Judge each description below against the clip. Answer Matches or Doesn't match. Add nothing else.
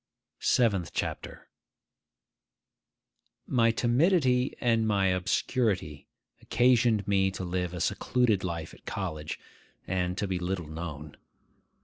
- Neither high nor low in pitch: Doesn't match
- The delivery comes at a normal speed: Doesn't match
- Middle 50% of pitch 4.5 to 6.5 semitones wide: Matches